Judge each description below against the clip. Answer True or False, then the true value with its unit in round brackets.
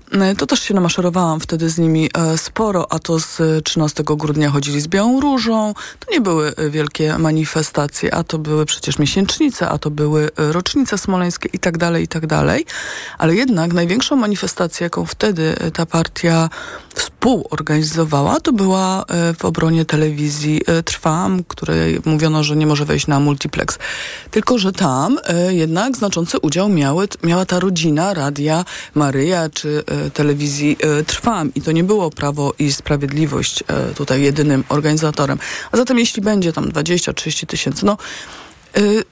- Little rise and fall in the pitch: False (3.6 semitones)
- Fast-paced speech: False (145 wpm)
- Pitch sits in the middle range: True (165 Hz)